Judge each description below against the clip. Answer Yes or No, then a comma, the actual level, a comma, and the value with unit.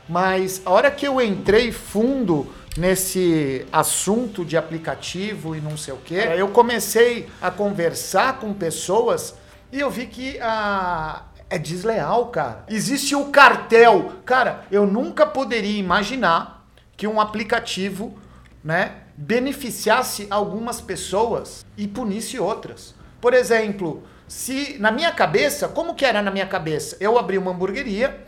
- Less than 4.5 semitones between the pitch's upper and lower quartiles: No, average, 4.8 semitones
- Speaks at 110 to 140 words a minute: Yes, average, 135 wpm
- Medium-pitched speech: No, high, 210 Hz